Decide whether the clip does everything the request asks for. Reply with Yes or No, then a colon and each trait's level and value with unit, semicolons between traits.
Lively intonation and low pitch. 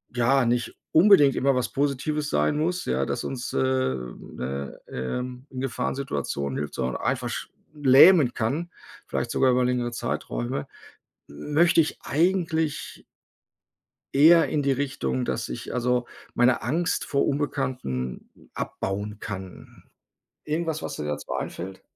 Yes: wide, 7.6 semitones; low, 130 Hz